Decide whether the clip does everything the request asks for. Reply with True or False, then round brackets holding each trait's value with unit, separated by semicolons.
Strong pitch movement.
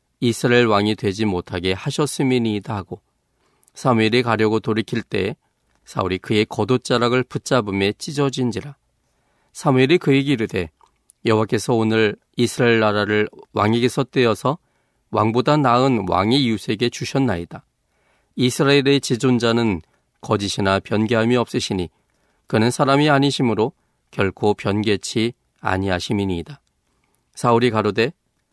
False (3.4 semitones)